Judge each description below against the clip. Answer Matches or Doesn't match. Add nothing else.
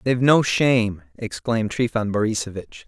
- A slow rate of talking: Matches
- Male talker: Matches